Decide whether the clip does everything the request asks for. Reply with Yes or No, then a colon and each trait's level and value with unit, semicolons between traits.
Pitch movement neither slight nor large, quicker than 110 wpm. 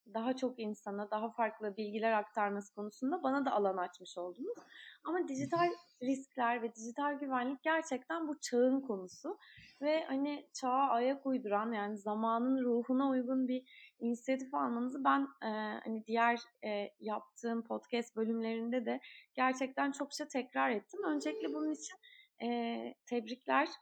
Yes: average, 4.0 semitones; average, 135 wpm